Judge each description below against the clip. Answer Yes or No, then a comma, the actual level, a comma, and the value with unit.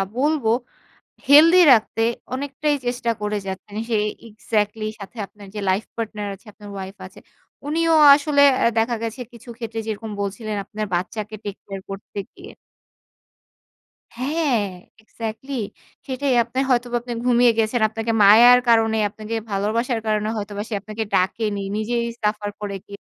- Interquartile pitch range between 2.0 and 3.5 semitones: Yes, average, 2.9 semitones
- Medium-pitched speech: No, high, 225 Hz